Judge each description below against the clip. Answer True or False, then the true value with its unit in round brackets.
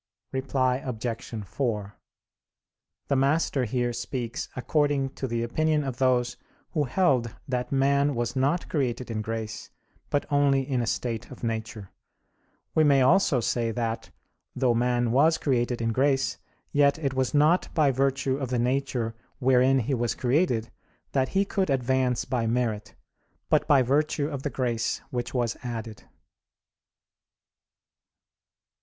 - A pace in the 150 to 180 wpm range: False (140 wpm)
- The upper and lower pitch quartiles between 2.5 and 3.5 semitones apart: True (2.8 semitones)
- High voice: False (130 Hz)